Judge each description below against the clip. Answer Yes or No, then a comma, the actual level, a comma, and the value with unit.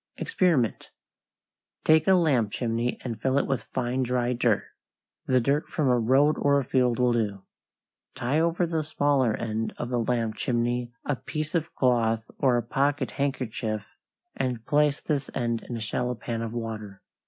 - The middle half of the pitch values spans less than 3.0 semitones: No, average, 3.6 semitones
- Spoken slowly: No, average, 170 wpm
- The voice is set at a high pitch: No, low, 125 Hz